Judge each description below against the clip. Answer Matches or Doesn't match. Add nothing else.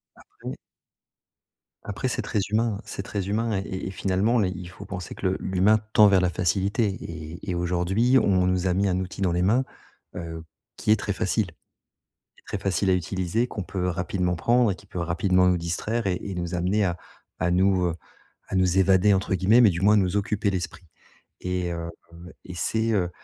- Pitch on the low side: Matches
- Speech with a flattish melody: Matches